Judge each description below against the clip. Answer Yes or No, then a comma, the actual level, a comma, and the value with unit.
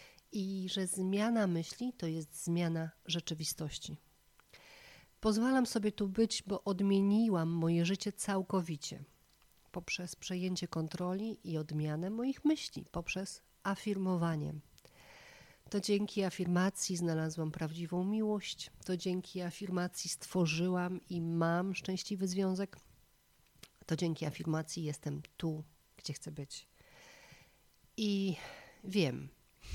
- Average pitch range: Yes, average, 3.2 semitones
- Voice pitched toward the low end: No, medium, 180 Hz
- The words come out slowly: Yes, slow, 100 wpm